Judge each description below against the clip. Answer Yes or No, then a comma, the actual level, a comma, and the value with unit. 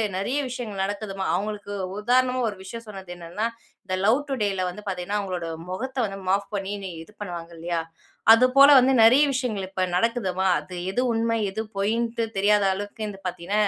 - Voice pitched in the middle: No, high, 205 Hz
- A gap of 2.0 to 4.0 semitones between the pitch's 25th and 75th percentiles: Yes, average, 3.2 semitones